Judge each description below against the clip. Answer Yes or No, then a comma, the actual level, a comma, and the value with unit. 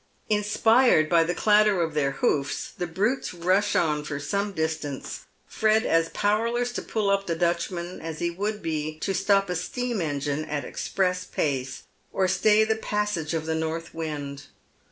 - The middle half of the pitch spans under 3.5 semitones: No, average, 4.9 semitones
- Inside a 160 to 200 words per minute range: Yes, average, 175 wpm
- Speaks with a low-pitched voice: No, medium, 175 Hz